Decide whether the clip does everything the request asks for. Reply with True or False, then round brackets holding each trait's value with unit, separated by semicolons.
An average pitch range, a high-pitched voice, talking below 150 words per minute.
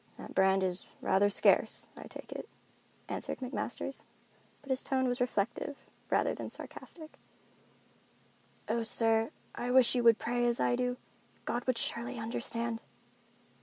False (1.9 semitones; 240 Hz; 140 wpm)